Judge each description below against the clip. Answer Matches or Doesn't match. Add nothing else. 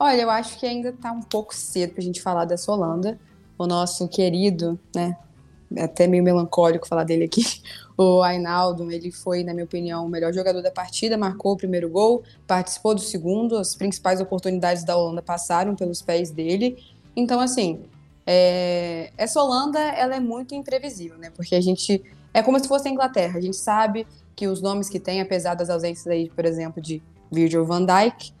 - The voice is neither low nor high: Matches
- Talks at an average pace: Doesn't match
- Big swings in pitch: Doesn't match